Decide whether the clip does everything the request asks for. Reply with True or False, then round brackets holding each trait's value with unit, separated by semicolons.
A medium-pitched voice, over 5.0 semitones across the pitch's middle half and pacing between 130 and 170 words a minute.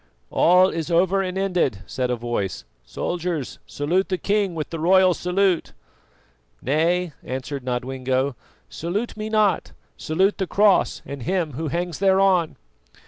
True (175 Hz; 5.5 semitones; 140 wpm)